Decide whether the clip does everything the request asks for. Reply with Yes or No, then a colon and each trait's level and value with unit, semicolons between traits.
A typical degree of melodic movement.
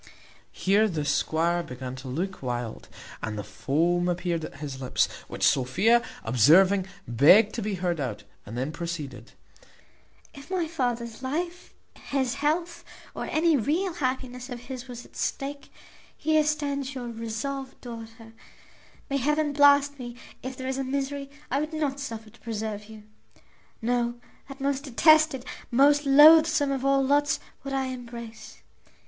No: wide, 7.3 semitones